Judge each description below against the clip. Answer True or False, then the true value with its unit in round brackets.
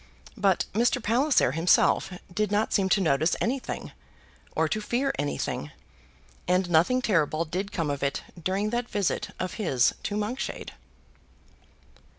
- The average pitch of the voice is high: True (195 Hz)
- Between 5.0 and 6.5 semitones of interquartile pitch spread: True (5.3 semitones)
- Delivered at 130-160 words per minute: True (140 wpm)